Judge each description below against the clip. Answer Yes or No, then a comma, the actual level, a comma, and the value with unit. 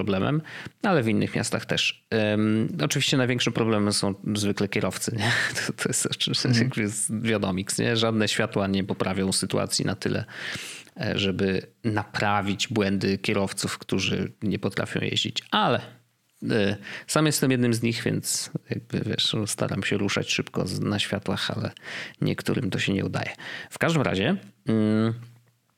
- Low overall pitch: Yes, low, 110 Hz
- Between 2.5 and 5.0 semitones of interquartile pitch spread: Yes, average, 3.1 semitones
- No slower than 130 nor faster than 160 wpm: Yes, average, 135 wpm